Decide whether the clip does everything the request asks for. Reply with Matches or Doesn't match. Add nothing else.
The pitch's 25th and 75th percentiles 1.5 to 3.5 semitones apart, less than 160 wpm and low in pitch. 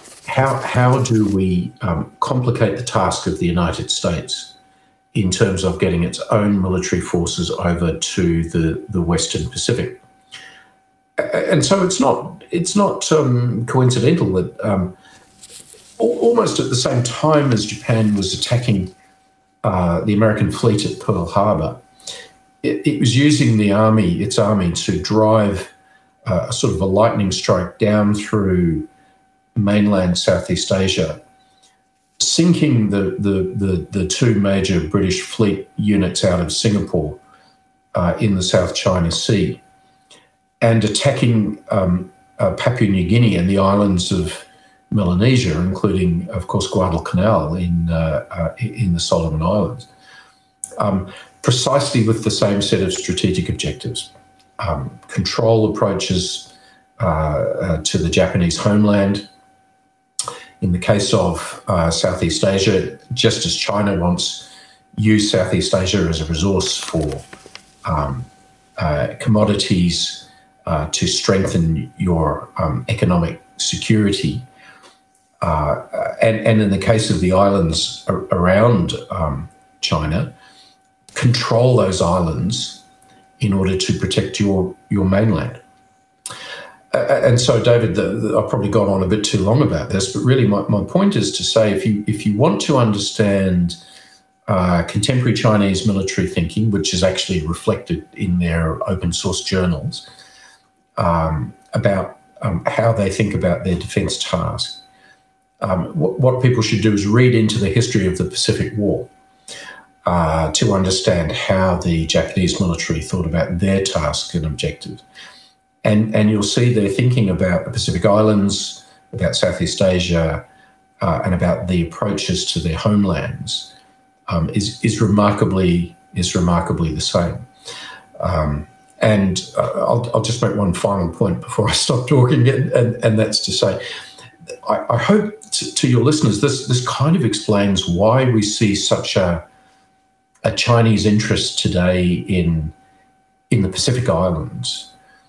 Doesn't match